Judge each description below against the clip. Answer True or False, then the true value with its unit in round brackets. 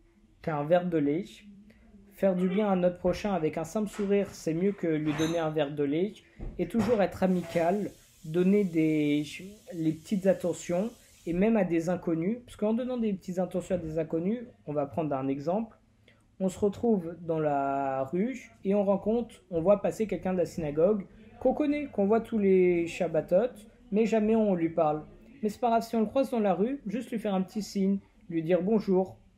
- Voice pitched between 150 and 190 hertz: True (185 Hz)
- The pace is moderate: True (200 wpm)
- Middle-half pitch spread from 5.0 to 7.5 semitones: False (4.5 semitones)